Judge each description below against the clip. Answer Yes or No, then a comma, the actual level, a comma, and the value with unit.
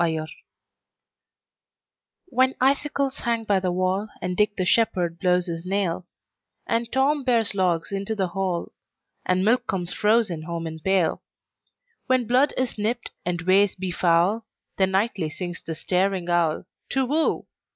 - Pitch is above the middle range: Yes, high, 195 Hz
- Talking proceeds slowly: Yes, slow, 130 wpm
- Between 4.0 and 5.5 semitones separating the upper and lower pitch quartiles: Yes, average, 4.8 semitones